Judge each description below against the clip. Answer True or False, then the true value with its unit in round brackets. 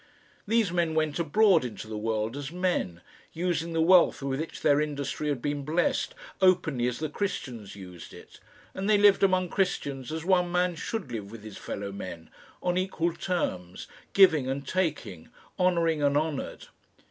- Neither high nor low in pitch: True (155 Hz)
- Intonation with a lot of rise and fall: True (6.4 semitones)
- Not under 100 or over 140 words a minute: False (170 wpm)